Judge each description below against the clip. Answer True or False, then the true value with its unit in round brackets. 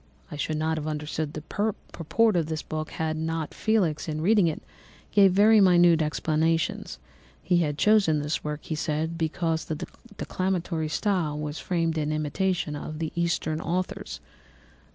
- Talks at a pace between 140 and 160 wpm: True (155 wpm)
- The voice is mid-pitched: True (160 Hz)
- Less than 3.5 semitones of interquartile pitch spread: True (2.5 semitones)